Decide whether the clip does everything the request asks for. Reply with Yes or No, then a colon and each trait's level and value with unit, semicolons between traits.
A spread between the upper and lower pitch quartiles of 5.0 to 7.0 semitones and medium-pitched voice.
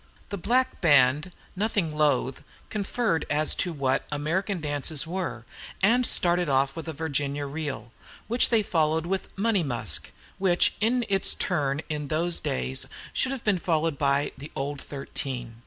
Yes: wide, 5.4 semitones; medium, 155 Hz